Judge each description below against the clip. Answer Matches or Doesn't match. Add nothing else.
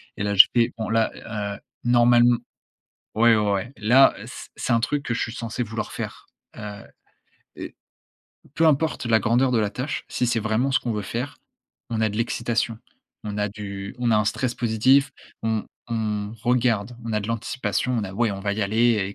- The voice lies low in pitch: Matches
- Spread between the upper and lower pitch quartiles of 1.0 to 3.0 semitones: Matches